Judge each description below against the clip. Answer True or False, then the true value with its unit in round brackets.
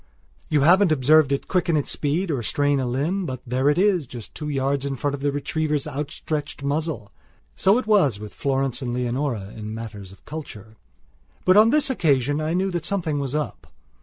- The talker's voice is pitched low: False (145 Hz)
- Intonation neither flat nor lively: True (3.7 semitones)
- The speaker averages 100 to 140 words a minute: False (195 wpm)